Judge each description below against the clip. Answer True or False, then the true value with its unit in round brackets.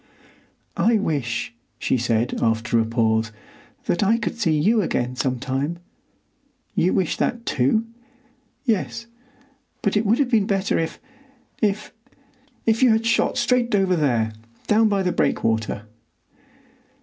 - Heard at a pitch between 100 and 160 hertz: False (190 Hz)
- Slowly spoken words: True (115 wpm)